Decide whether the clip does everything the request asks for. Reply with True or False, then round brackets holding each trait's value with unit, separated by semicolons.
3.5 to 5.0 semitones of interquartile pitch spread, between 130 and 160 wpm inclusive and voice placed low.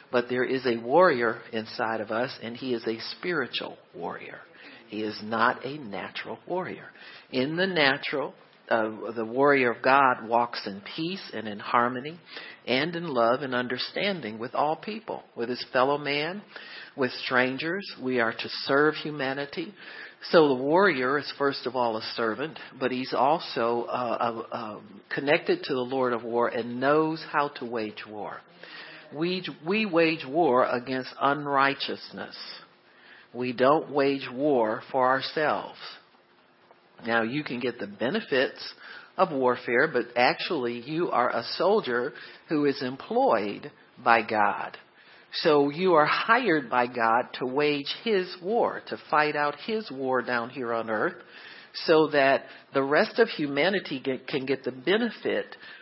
True (4.1 semitones; 150 wpm; 130 Hz)